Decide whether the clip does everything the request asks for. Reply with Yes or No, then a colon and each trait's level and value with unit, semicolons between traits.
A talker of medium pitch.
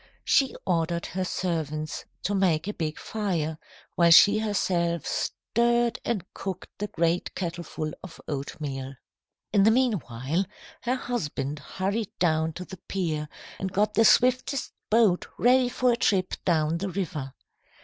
Yes: medium, 180 Hz